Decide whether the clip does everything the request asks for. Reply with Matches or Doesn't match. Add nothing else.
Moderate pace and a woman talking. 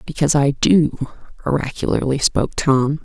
Doesn't match